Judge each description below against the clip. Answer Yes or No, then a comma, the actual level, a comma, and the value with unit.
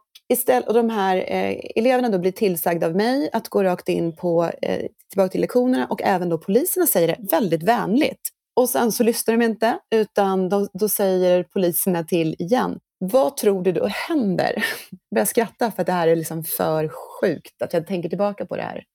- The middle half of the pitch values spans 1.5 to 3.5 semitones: No, average, 4.8 semitones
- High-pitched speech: Yes, high, 195 Hz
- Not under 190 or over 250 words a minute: Yes, fast, 195 wpm